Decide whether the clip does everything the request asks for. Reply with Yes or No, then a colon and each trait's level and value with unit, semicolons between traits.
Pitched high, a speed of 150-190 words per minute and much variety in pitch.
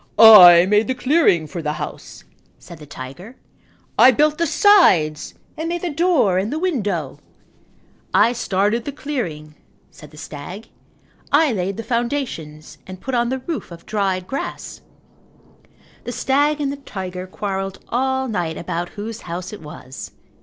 Yes: high, 210 Hz; average, 155 wpm; wide, 7.3 semitones